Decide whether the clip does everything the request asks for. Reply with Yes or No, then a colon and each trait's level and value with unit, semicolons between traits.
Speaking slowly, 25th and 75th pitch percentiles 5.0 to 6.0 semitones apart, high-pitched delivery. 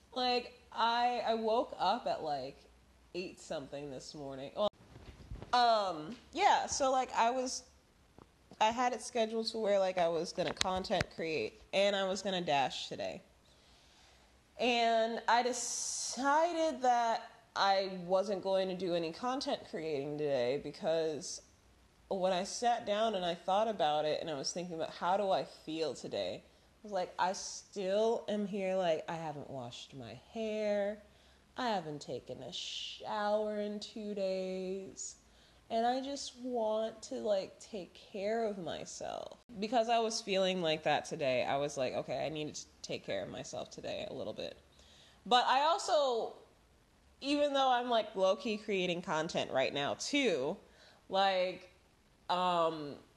No: average, 155 wpm; average, 5.3 semitones; high, 200 Hz